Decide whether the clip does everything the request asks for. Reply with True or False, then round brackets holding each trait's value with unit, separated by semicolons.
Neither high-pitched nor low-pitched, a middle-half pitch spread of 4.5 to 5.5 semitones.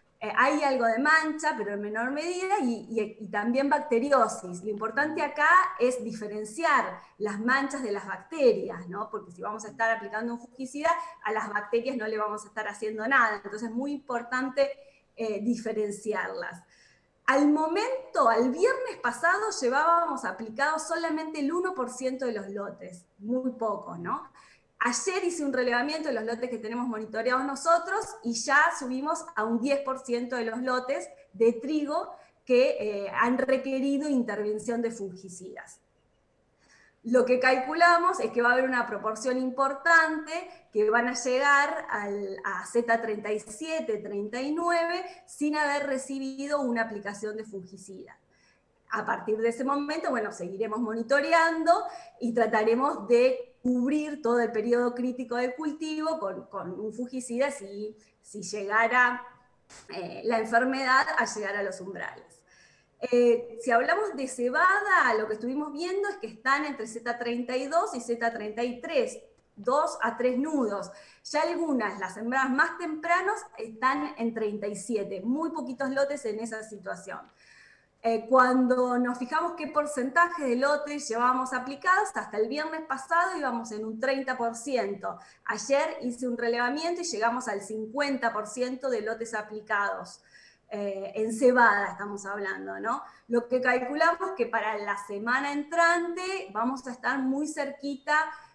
False (250 Hz; 5.2 semitones)